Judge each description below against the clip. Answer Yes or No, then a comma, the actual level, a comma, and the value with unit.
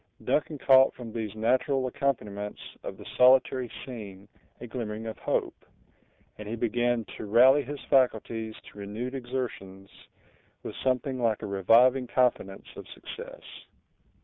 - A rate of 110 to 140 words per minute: Yes, slow, 135 wpm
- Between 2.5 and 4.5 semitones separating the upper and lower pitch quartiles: Yes, average, 3.2 semitones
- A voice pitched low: Yes, low, 120 Hz